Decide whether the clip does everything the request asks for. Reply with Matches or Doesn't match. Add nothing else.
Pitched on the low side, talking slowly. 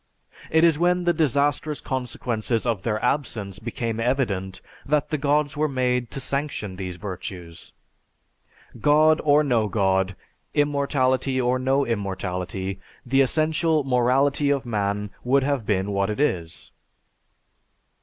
Matches